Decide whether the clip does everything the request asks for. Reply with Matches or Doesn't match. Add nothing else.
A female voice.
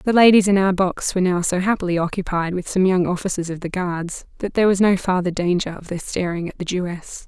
Matches